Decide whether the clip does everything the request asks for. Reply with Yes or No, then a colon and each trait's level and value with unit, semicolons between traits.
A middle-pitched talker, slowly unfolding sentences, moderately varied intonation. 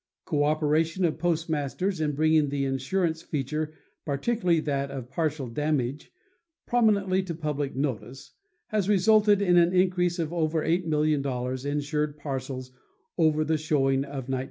Yes: medium, 155 Hz; slow, 130 wpm; average, 3.8 semitones